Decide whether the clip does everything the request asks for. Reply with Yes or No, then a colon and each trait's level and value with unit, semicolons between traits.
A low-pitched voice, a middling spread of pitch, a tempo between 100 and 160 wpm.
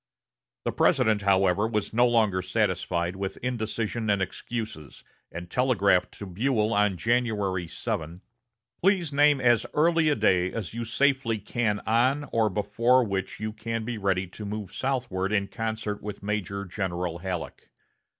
Yes: low, 105 Hz; average, 3.7 semitones; average, 150 wpm